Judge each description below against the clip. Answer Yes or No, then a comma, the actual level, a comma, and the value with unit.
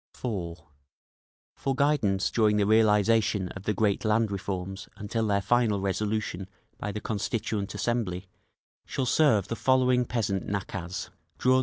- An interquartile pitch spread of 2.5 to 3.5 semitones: Yes, average, 2.9 semitones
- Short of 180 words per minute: Yes, average, 140 wpm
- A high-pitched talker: No, low, 105 Hz